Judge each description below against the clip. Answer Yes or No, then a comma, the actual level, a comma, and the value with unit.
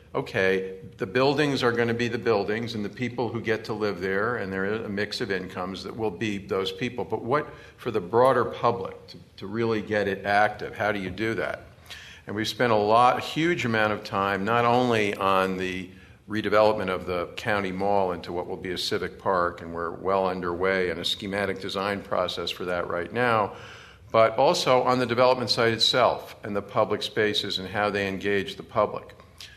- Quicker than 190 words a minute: Yes, fast, 205 wpm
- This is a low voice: Yes, low, 105 Hz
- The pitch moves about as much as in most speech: Yes, average, 3.3 semitones